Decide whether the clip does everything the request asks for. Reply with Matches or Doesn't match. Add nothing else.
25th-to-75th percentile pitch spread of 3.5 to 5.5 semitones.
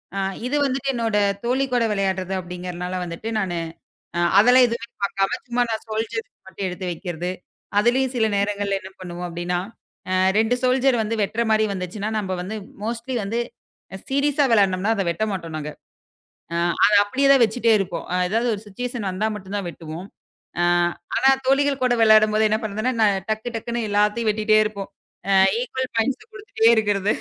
Matches